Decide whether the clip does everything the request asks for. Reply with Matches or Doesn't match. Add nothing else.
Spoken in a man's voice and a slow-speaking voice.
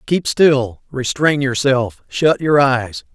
Matches